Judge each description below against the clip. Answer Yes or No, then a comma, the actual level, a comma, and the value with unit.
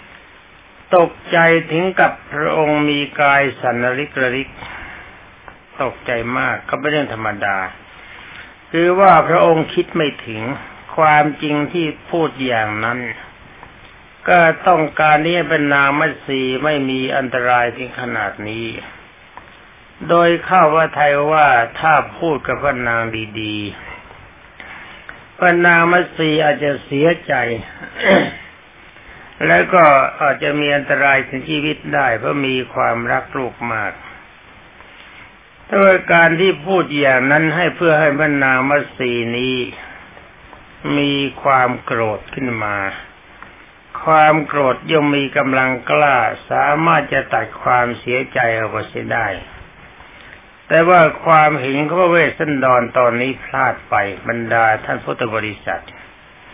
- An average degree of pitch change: Yes, average, 4.1 semitones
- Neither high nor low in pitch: Yes, medium, 145 Hz